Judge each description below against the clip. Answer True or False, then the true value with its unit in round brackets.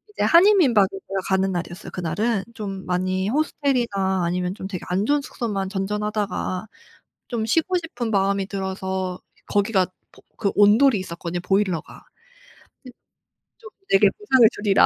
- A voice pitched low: False (200 Hz)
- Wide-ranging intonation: False (3.7 semitones)